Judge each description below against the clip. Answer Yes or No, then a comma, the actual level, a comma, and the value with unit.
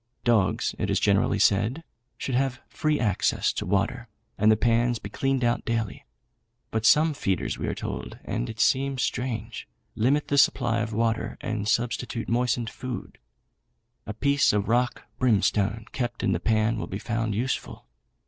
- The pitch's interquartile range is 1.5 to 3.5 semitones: Yes, average, 2.8 semitones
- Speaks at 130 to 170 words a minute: Yes, average, 165 wpm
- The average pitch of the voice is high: No, low, 115 Hz